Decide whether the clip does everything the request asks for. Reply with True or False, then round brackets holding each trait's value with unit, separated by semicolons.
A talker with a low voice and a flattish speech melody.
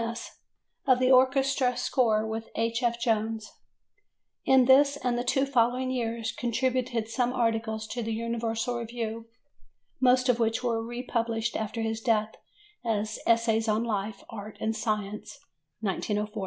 False (230 Hz; 2.0 semitones)